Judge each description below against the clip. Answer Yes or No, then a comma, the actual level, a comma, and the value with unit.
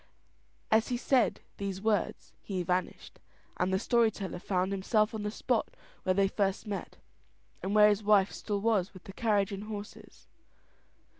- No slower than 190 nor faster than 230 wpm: No, average, 165 wpm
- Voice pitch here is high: Yes, high, 205 Hz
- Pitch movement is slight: Yes, narrow, 2.0 semitones